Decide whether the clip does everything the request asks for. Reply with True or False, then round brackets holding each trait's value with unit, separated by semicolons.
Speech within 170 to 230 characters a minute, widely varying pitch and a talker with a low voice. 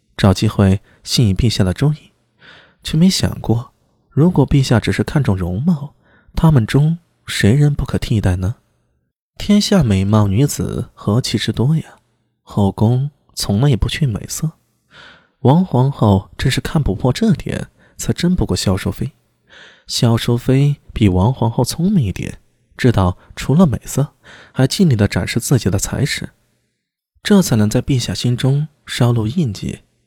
True (220 characters per minute; 6.1 semitones; 120 Hz)